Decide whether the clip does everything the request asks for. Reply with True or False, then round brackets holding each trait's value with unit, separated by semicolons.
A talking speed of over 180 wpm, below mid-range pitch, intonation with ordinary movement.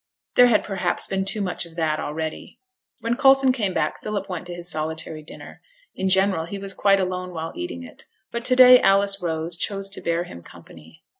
False (205 wpm; 185 Hz; 3.7 semitones)